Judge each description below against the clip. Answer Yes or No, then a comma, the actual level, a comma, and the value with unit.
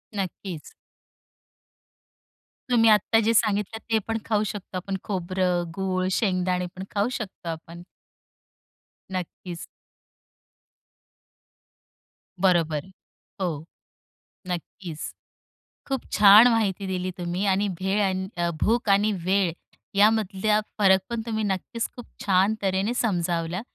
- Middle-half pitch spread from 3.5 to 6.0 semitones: No, average, 2.8 semitones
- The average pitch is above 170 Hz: Yes, high, 190 Hz